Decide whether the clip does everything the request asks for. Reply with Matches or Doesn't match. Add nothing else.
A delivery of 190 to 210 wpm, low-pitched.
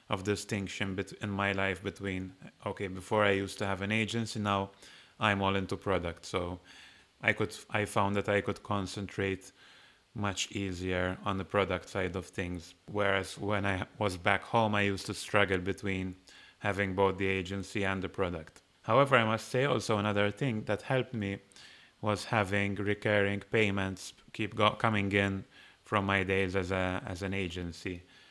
Doesn't match